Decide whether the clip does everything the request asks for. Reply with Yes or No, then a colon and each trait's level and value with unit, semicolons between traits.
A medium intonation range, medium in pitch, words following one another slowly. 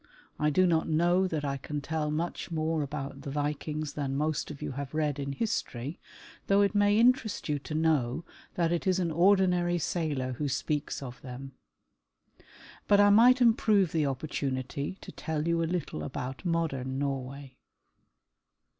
No: average, 4.0 semitones; medium, 155 Hz; average, 165 wpm